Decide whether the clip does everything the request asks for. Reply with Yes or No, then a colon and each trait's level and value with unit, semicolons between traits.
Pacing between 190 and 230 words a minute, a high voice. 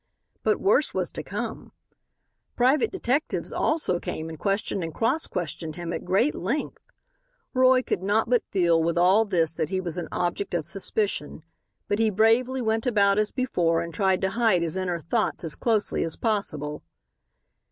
No: average, 175 wpm; high, 195 Hz